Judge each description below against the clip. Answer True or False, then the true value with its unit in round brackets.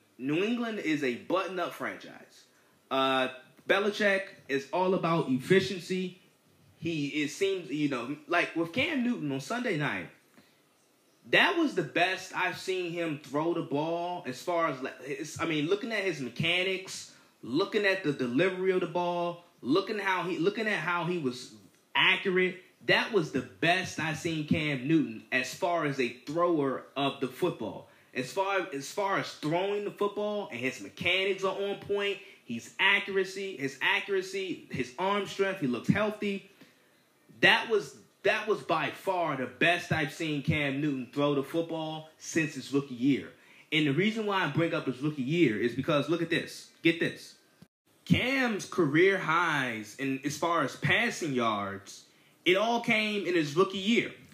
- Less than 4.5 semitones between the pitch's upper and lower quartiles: False (5.3 semitones)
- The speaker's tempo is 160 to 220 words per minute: True (170 wpm)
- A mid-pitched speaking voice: True (170 Hz)